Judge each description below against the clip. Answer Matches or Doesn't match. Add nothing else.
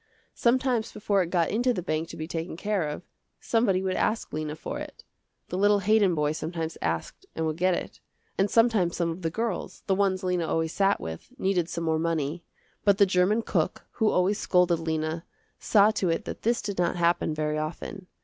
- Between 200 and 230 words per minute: Matches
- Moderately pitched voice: Matches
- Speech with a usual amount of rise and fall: Matches